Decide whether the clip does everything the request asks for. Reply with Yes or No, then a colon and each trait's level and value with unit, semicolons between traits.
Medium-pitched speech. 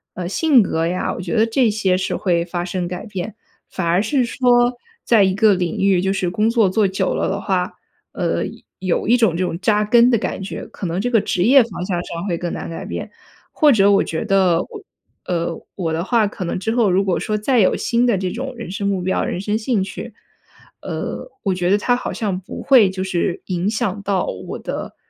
No: high, 195 Hz